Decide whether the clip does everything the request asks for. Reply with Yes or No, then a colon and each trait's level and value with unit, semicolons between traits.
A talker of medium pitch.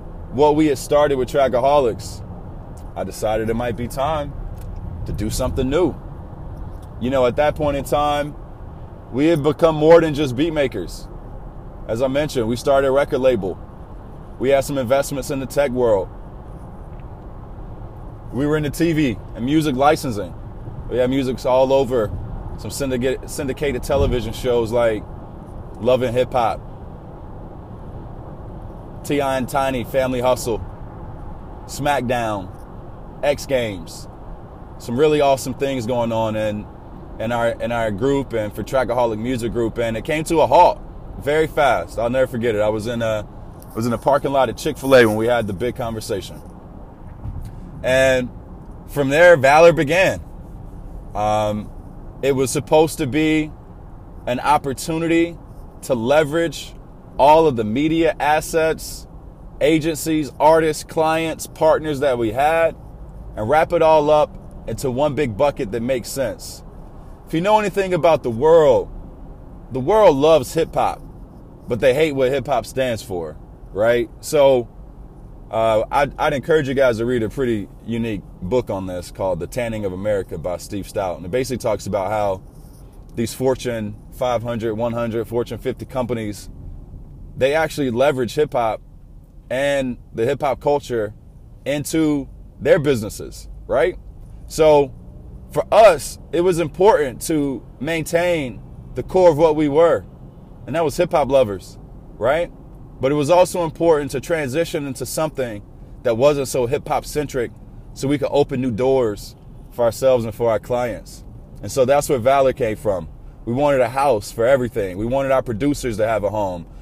No: low, 130 Hz